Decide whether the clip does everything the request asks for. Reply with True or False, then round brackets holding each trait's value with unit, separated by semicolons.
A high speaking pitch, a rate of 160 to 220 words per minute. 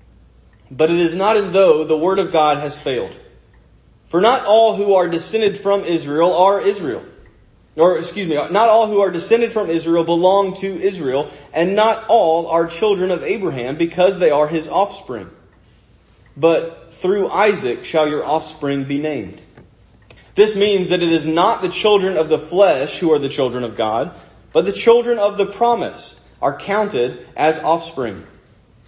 False (170 Hz; 170 wpm)